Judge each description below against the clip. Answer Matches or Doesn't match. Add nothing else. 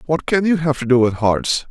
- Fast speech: Matches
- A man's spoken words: Matches